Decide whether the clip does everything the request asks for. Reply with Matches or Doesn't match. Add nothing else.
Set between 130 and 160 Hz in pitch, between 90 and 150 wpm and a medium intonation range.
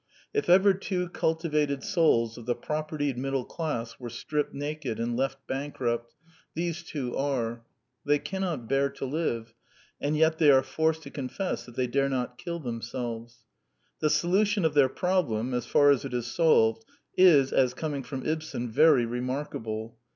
Doesn't match